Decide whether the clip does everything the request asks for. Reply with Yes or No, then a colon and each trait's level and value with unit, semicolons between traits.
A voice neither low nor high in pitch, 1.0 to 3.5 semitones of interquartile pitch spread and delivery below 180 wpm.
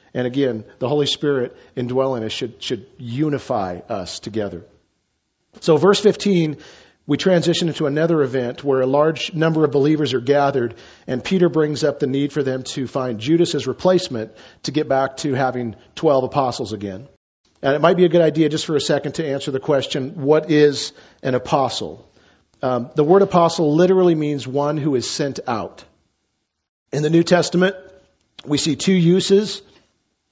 No: medium, 145 Hz; average, 3.9 semitones; average, 170 wpm